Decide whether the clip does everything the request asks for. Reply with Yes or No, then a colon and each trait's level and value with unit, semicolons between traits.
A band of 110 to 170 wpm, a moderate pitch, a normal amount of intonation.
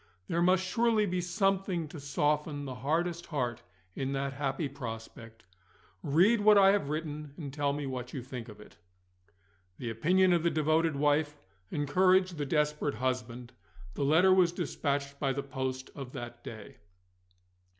Yes: average, 160 wpm; medium, 145 Hz; average, 4.6 semitones